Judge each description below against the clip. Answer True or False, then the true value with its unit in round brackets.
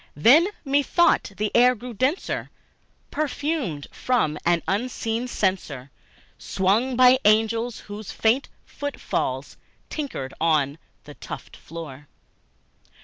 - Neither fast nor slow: False (95 wpm)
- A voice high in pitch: True (220 Hz)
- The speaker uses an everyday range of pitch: False (7.6 semitones)